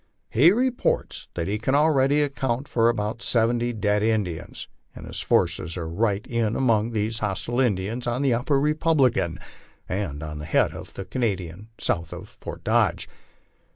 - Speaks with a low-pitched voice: Yes, low, 115 Hz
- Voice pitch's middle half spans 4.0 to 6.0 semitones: Yes, average, 4.9 semitones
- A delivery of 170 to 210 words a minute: No, average, 160 wpm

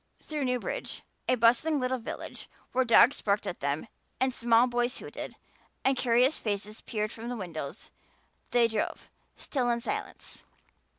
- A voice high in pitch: Yes, high, 240 Hz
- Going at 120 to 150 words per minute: Yes, average, 145 wpm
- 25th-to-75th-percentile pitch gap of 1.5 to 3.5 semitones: Yes, average, 2.8 semitones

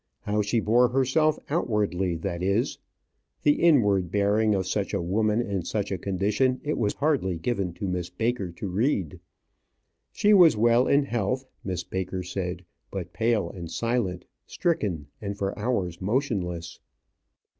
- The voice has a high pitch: No, low, 100 Hz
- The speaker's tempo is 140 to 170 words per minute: Yes, average, 150 wpm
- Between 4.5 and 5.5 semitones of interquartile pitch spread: Yes, average, 4.8 semitones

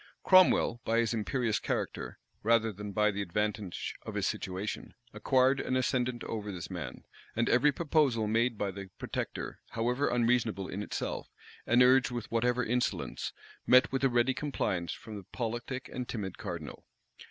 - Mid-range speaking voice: No, low, 115 Hz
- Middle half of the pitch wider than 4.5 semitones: No, average, 3.3 semitones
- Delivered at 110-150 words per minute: No, average, 160 wpm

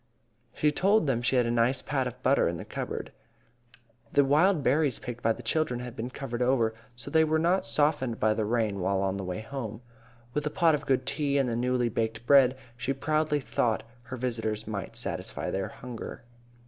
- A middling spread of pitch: Yes, average, 3.9 semitones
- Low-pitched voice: Yes, low, 125 Hz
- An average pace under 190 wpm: No, fast, 205 wpm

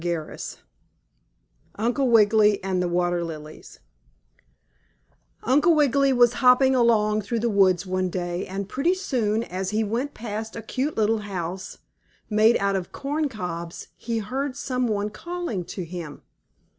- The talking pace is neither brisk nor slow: Yes, average, 145 wpm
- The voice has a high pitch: Yes, high, 215 Hz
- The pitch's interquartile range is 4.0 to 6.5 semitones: Yes, average, 5.3 semitones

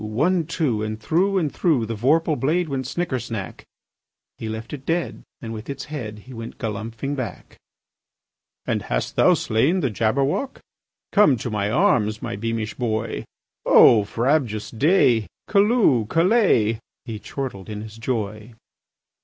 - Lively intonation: Yes, wide, 5.9 semitones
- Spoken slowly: No, average, 145 wpm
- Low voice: Yes, low, 120 Hz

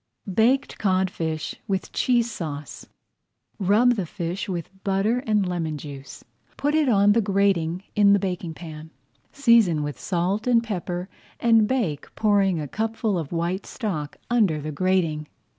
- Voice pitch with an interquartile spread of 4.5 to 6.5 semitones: Yes, average, 4.9 semitones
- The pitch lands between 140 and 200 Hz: Yes, high, 190 Hz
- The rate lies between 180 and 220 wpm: No, average, 145 wpm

